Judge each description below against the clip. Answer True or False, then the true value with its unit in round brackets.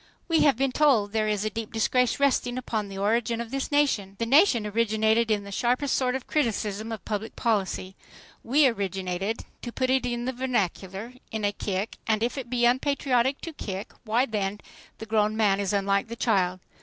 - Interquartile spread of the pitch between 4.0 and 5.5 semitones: False (3.6 semitones)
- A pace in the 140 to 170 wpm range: False (195 wpm)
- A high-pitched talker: True (225 Hz)